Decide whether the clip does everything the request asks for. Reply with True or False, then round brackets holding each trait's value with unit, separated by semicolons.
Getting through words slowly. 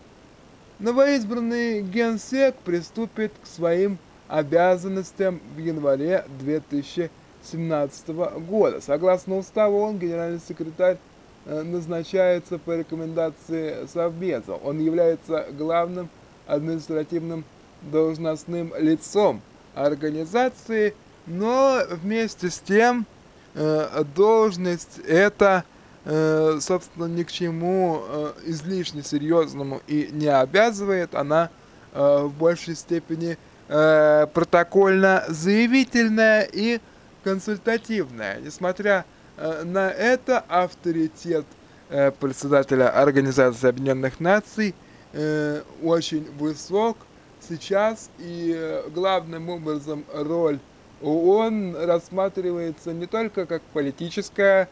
True (75 wpm)